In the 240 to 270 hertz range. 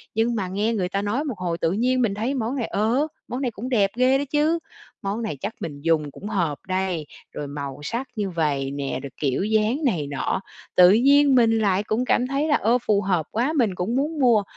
No: high, 215 Hz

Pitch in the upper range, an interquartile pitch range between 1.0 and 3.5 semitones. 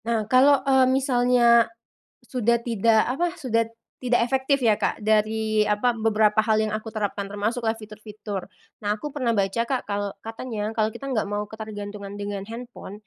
Yes: high, 220 Hz; average, 2.7 semitones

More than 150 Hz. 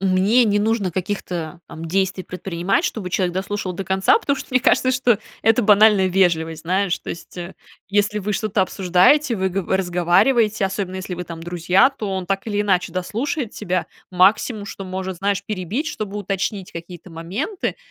Yes: high, 190 Hz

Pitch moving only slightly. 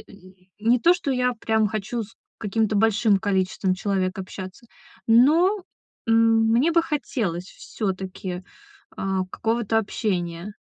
No: average, 3.5 semitones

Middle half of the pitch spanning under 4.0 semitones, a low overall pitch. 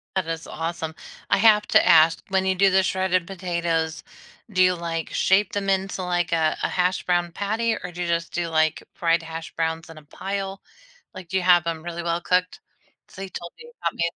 No: narrow, 2.4 semitones; medium, 175 Hz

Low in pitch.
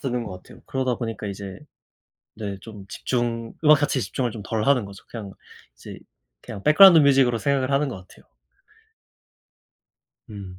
Yes: low, 115 Hz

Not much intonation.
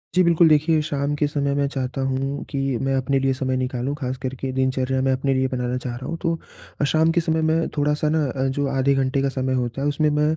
Yes: narrow, 2.2 semitones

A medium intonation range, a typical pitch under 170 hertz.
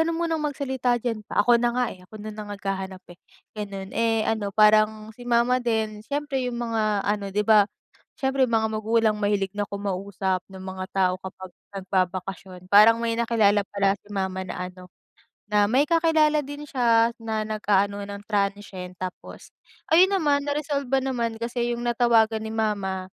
No: average, 3.3 semitones; high, 215 Hz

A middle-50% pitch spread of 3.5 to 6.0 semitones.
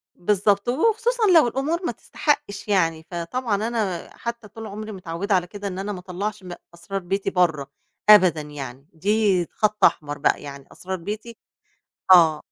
Yes: average, 4.1 semitones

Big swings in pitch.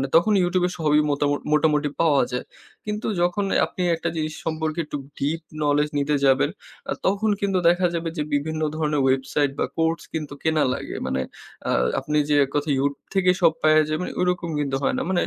No: average, 2.9 semitones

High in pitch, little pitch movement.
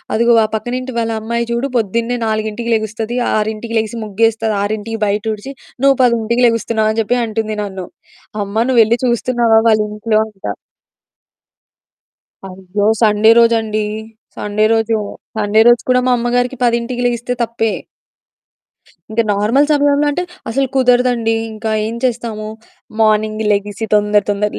Yes: high, 225 Hz; narrow, 1.9 semitones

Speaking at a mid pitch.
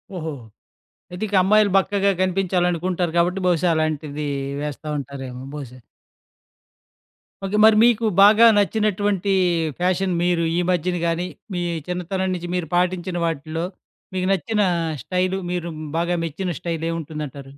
Yes: medium, 180 Hz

